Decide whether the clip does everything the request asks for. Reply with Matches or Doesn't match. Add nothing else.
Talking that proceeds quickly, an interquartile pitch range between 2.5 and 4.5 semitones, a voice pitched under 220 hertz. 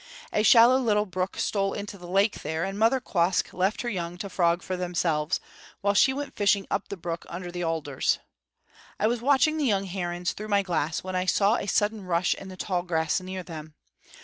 Matches